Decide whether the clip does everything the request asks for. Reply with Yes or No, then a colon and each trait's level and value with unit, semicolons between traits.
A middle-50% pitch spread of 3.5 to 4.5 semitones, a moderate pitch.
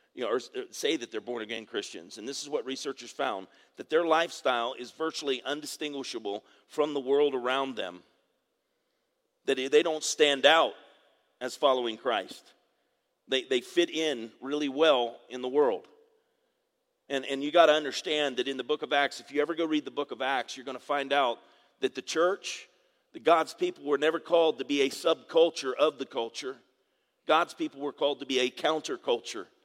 Yes: average, 4.0 semitones; medium, 150 Hz